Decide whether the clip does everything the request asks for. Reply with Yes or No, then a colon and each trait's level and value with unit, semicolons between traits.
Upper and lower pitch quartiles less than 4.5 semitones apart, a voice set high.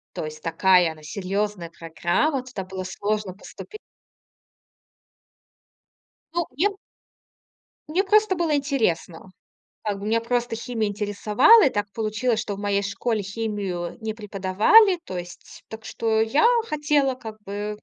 No: average, 4.8 semitones; high, 210 Hz